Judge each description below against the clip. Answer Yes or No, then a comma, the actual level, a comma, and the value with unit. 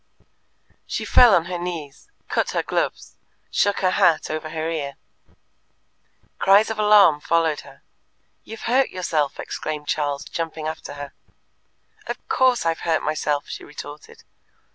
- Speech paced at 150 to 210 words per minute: No, average, 140 wpm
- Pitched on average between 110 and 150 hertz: No, medium, 165 Hz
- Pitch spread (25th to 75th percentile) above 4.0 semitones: Yes, average, 4.4 semitones